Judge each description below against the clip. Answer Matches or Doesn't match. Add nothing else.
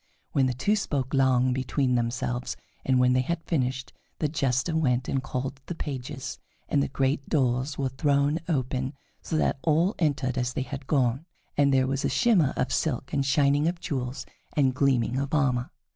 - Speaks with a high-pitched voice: Doesn't match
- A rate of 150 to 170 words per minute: Doesn't match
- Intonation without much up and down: Matches